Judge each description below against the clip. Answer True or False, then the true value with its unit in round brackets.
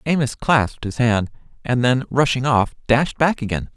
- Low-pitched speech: True (125 Hz)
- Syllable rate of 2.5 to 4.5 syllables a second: False (4.8 syllables/s)